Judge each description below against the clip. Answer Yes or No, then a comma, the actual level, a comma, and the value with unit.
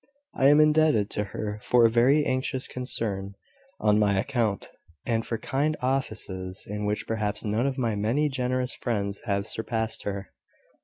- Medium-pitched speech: No, low, 115 Hz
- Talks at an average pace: Yes, average, 160 wpm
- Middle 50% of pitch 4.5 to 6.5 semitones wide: No, average, 4.0 semitones